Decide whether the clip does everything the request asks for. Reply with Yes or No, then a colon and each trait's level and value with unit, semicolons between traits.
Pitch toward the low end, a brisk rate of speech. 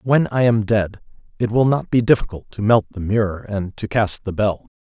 Yes: low, 110 Hz; fast, 225 wpm